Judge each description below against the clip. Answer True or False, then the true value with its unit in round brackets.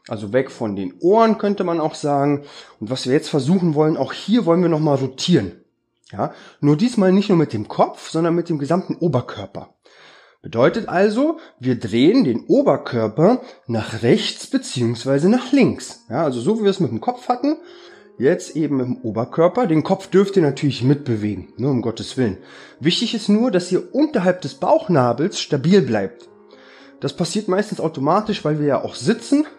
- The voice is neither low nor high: True (165 Hz)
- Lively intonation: True (7.3 semitones)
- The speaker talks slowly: False (185 wpm)